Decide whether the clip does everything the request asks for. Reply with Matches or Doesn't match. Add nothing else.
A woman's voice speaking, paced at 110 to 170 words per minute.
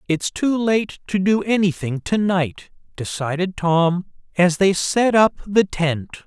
Doesn't match